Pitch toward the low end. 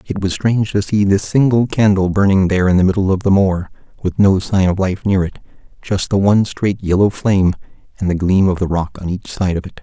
Yes: very low, 95 Hz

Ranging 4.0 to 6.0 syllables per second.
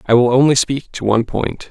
Yes: 5.7 syllables/s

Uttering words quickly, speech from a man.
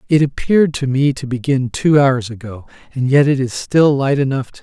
Yes: fast, 235 wpm; male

